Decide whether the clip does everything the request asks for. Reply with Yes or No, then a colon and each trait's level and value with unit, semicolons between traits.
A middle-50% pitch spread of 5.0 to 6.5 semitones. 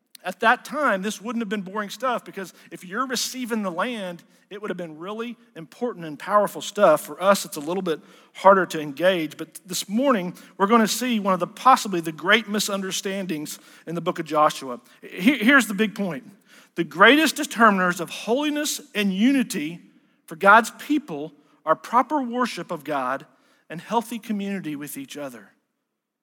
Yes: wide, 5.5 semitones